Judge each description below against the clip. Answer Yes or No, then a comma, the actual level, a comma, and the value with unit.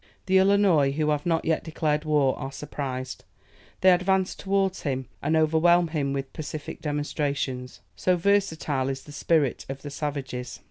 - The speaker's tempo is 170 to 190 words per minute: No, average, 155 wpm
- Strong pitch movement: No, average, 3.9 semitones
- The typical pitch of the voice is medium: Yes, medium, 150 Hz